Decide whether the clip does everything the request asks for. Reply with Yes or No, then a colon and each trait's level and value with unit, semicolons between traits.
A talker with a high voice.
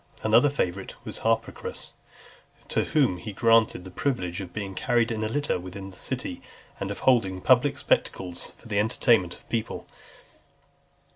No: low, 110 Hz